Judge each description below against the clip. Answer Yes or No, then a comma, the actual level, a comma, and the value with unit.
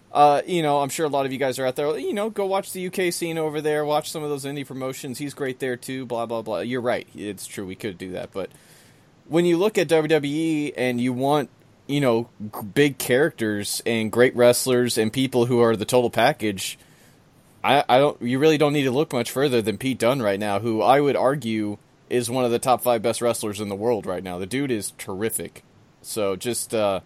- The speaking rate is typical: No, fast, 235 wpm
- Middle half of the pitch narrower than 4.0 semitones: No, average, 4.7 semitones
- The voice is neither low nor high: No, low, 125 Hz